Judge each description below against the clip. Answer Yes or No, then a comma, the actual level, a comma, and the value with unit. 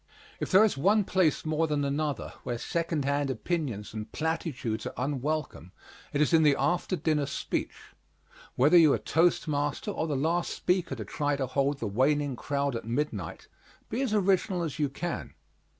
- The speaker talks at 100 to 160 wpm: No, average, 180 wpm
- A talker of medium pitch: Yes, medium, 145 Hz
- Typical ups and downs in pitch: Yes, average, 3.6 semitones